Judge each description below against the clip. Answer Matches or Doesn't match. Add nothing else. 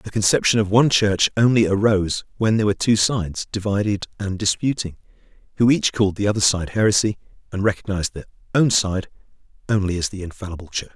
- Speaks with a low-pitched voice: Matches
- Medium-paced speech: Matches